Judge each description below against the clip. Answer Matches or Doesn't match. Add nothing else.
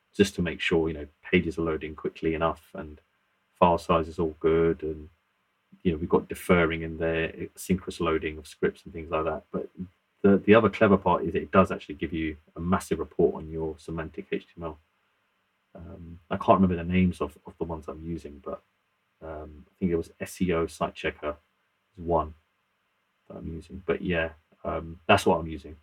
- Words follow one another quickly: Doesn't match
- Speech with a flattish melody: Matches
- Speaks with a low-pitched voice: Matches